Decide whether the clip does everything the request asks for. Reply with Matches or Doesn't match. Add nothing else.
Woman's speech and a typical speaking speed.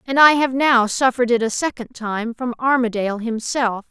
Matches